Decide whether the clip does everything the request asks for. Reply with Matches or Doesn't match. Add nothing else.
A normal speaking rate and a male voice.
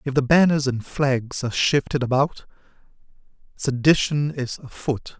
Doesn't match